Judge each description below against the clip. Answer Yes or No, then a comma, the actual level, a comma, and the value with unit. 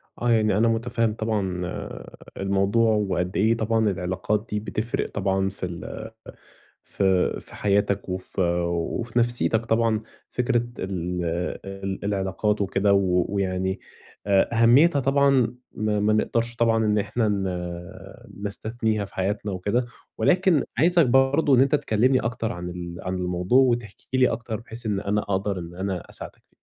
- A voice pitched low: Yes, low, 105 Hz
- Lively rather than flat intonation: No, average, 3.4 semitones